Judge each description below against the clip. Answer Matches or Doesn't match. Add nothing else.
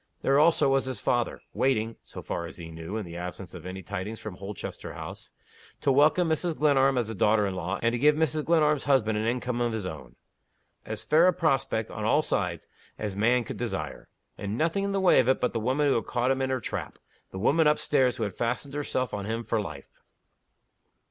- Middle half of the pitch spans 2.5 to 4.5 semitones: Doesn't match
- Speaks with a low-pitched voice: Matches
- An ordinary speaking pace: Doesn't match